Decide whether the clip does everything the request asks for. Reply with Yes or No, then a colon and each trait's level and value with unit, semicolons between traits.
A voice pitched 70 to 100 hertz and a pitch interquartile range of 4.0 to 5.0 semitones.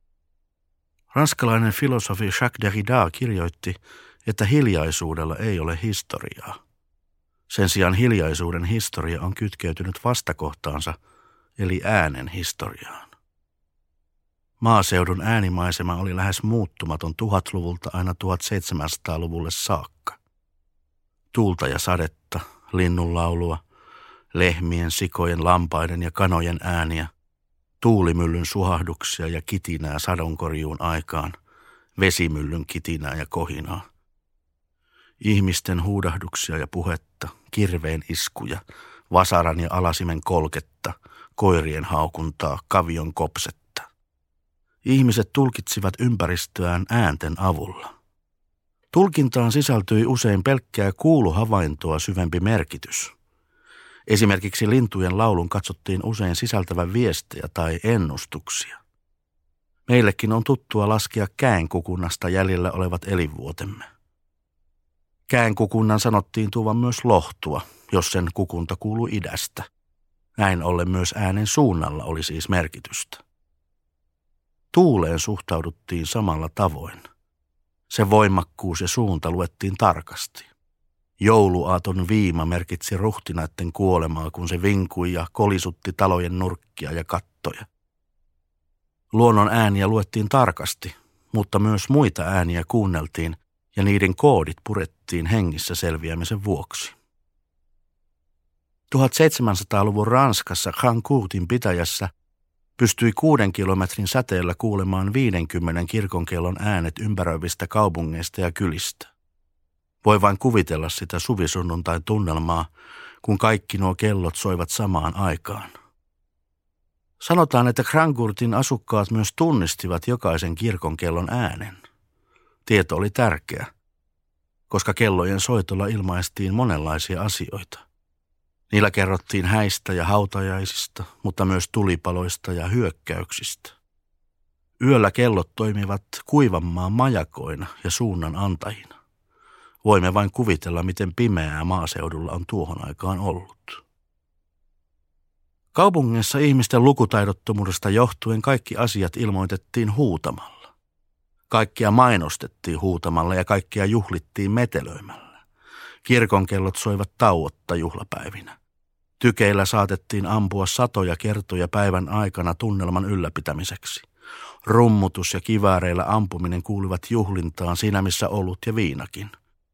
Yes: very low, 90 Hz; average, 4.6 semitones